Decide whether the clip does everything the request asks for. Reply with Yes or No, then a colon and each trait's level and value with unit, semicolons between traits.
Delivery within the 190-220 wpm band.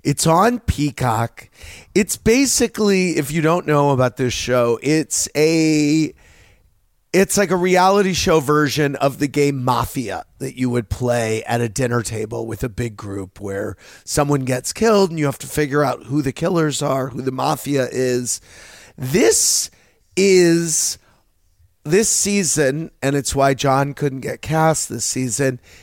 No: average, 155 wpm